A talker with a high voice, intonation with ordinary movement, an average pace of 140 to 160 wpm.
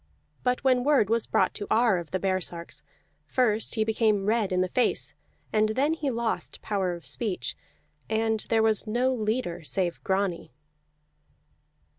Yes: high, 215 Hz; average, 3.9 semitones; average, 155 wpm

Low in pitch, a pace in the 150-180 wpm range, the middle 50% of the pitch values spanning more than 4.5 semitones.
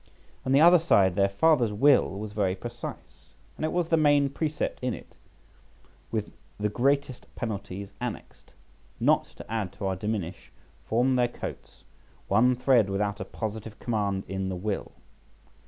Yes: low, 110 Hz; average, 155 wpm; average, 5.1 semitones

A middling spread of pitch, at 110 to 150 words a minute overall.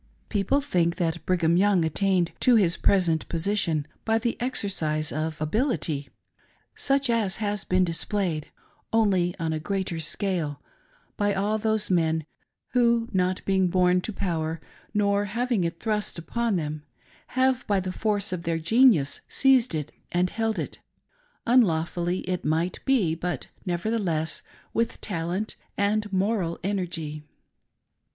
Yes: average, 4.6 semitones; average, 140 wpm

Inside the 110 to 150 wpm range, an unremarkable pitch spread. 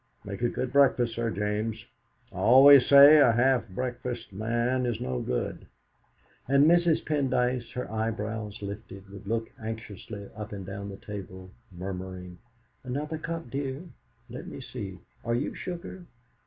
Yes: average, 145 wpm; average, 4.6 semitones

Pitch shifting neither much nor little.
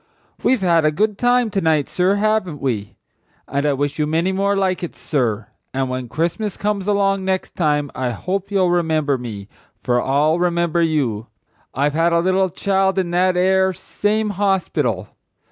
Yes: average, 5.0 semitones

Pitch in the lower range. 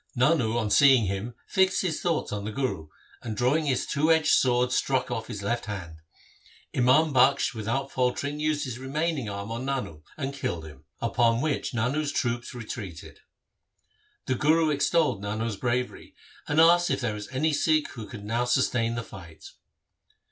Yes: low, 125 Hz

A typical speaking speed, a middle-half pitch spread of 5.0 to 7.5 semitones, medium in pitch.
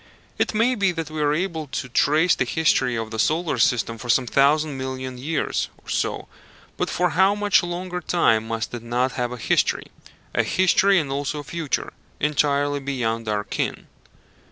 Yes: average, 180 wpm; average, 5.3 semitones; medium, 145 Hz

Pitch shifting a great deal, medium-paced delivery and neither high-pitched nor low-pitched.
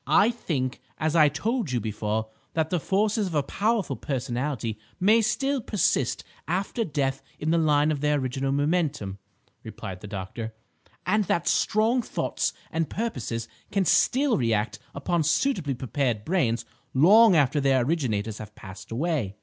Yes: wide, 7.7 semitones; average, 150 wpm; medium, 145 Hz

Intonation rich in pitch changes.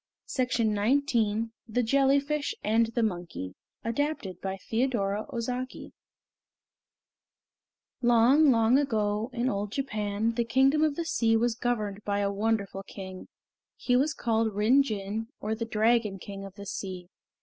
No: average, 3.6 semitones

